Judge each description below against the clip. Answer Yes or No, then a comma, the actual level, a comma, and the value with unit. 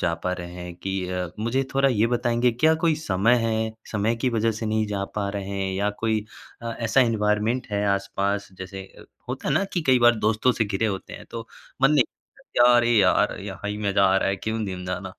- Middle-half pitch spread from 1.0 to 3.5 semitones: Yes, average, 3.1 semitones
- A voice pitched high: No, low, 105 Hz